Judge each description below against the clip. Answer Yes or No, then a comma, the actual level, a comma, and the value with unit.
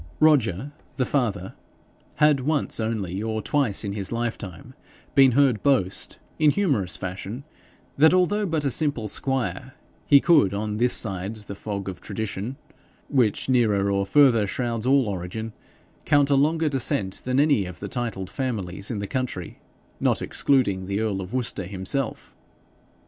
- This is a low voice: Yes, low, 115 Hz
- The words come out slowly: No, average, 155 wpm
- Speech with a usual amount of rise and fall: No, wide, 5.8 semitones